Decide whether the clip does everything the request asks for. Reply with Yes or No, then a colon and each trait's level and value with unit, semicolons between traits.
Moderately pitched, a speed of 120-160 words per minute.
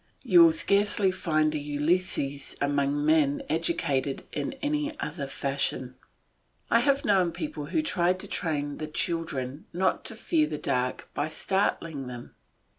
Yes: medium, 155 Hz; average, 145 wpm